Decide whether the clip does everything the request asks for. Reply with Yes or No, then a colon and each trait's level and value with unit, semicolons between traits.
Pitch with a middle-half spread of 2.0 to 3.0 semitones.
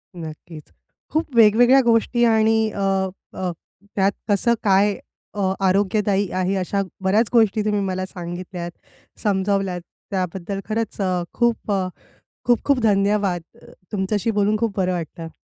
Yes: average, 2.7 semitones